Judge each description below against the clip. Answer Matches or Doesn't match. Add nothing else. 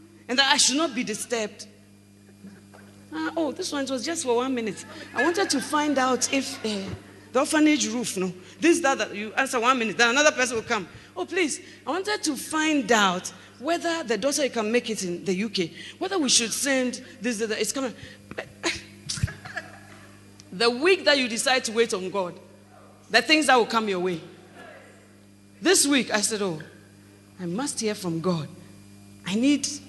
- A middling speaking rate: Matches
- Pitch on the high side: Matches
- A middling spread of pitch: Doesn't match